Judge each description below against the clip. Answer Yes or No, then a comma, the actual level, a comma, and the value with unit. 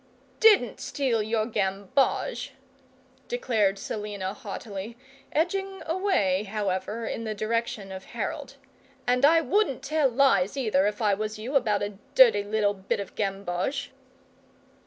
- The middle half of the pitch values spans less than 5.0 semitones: No, average, 5.3 semitones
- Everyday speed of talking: No, slow, 130 wpm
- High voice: Yes, high, 220 Hz